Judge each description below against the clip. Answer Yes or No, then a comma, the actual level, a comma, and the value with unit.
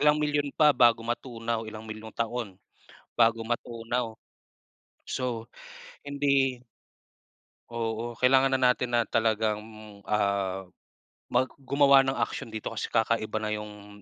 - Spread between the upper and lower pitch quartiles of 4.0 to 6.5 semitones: No, average, 2.9 semitones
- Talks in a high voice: No, low, 115 Hz